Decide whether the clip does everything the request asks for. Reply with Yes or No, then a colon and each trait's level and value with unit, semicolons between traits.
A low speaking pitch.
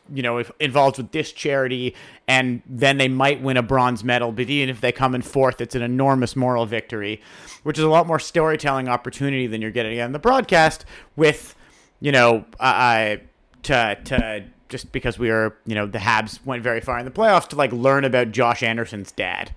Yes: low, 125 Hz